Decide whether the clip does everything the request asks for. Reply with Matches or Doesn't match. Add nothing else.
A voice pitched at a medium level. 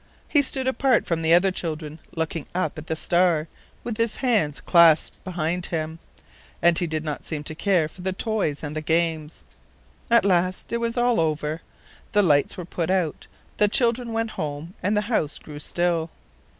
Matches